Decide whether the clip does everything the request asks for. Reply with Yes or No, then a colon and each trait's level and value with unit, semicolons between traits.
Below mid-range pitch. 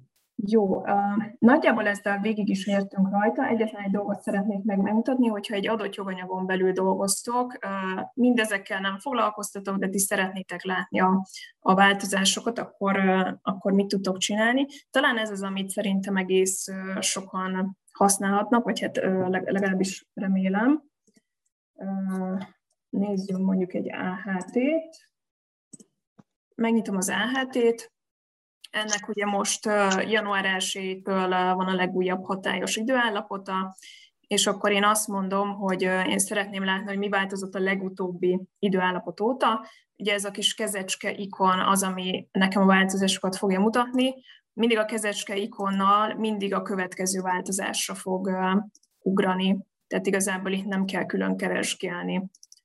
No: high, 200 Hz